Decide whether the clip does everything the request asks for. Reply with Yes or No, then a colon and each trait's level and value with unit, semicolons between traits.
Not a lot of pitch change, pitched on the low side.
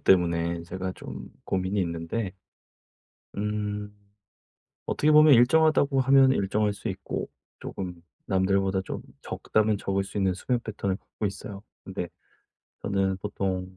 Yes: narrow, 2.3 semitones; low, 100 Hz